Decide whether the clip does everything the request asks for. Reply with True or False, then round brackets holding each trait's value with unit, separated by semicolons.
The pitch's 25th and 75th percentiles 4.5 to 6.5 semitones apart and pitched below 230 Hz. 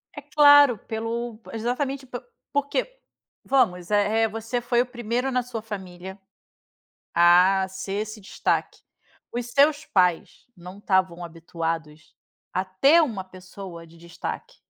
True (5.4 semitones; 215 Hz)